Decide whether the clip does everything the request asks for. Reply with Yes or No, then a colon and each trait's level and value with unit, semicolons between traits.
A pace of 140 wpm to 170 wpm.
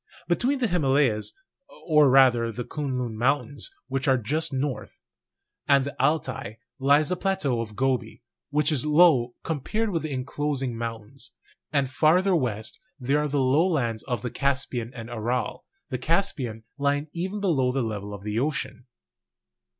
Yes: average, 160 wpm